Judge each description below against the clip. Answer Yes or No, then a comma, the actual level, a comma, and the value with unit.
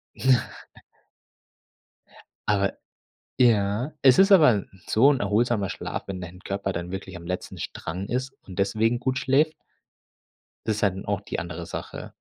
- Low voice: Yes, low, 105 Hz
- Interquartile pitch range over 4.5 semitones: Yes, average, 5.1 semitones